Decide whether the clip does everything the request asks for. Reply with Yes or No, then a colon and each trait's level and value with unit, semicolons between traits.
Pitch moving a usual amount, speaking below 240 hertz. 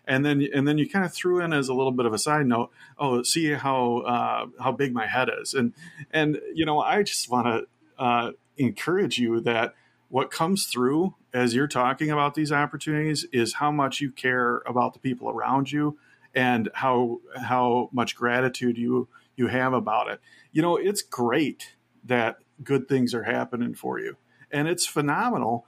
Yes: average, 3.4 semitones; low, 135 Hz